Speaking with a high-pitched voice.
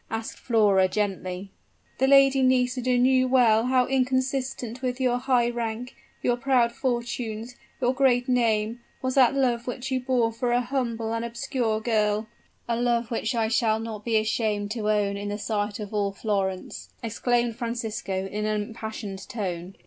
Yes: high, 235 Hz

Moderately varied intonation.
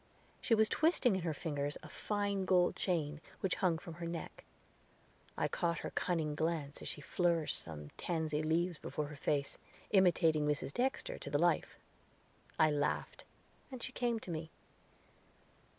Yes: average, 3.8 semitones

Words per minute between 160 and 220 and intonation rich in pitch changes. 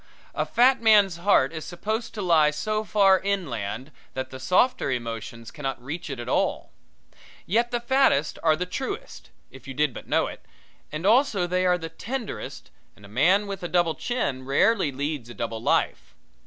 Yes: average, 180 wpm; wide, 7.9 semitones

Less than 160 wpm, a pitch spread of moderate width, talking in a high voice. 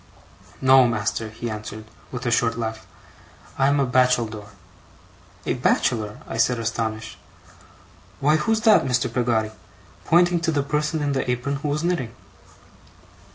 No: average, 140 wpm; average, 4.2 semitones; low, 125 Hz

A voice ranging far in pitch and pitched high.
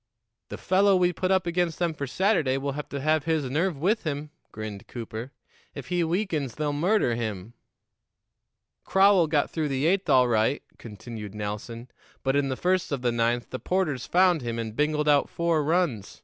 No: wide, 6.4 semitones; medium, 145 Hz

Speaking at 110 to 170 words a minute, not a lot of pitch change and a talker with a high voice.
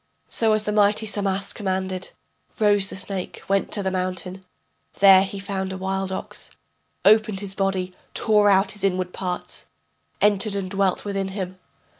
Yes: average, 160 wpm; narrow, 1.4 semitones; high, 195 Hz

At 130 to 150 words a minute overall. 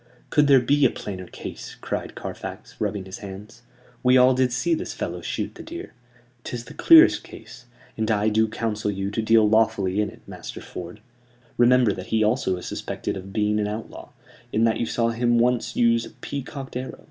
No: average, 195 wpm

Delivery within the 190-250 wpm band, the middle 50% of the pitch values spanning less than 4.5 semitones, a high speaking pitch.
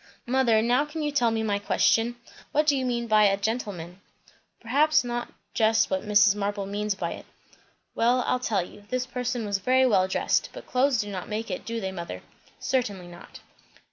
Yes: average, 195 wpm; average, 3.8 semitones; high, 225 Hz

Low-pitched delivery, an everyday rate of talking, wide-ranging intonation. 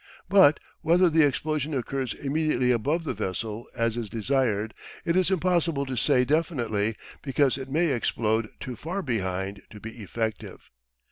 Yes: low, 130 Hz; average, 150 wpm; wide, 5.7 semitones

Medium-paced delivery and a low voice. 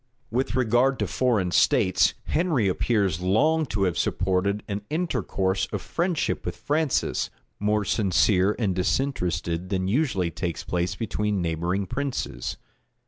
No: slow, 130 wpm; low, 100 Hz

